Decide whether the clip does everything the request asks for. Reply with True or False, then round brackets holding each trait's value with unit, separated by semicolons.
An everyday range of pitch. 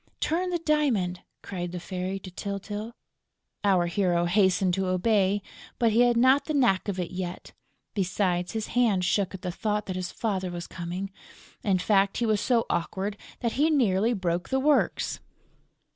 True (4.0 semitones)